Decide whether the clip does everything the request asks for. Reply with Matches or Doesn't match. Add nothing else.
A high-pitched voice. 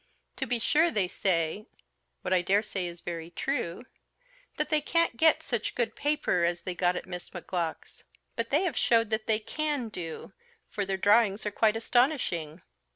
Matches